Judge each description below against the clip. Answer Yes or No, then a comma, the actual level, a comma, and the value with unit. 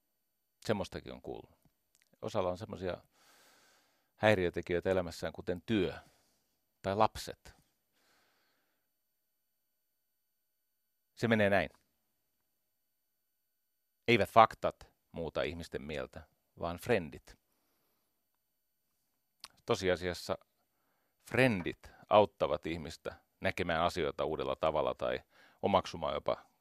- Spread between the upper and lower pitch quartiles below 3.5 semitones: No, average, 4.8 semitones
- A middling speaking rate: No, slow, 75 wpm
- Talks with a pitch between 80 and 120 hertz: Yes, low, 105 Hz